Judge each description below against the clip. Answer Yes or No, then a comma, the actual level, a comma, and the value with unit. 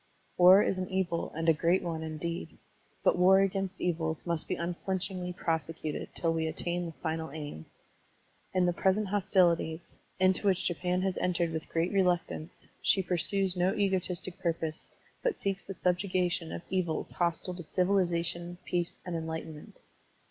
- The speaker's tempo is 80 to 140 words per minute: No, average, 160 wpm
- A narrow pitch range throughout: Yes, narrow, 2.3 semitones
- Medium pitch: Yes, medium, 175 Hz